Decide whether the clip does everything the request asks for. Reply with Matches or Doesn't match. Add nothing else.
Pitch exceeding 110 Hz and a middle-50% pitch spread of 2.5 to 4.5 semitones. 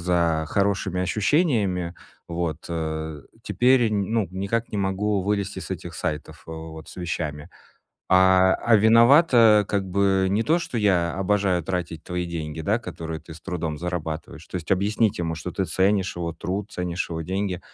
Doesn't match